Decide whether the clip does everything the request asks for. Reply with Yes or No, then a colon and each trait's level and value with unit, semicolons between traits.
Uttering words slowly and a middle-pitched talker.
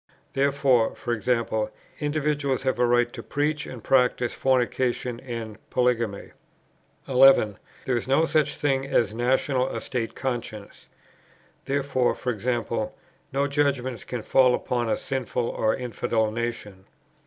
No: slow, 130 wpm; low, 125 Hz